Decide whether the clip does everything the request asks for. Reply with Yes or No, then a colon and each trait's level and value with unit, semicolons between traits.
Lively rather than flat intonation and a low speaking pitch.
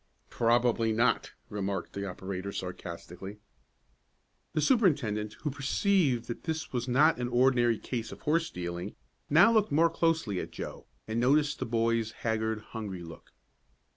Yes: wide, 6.1 semitones; low, 115 Hz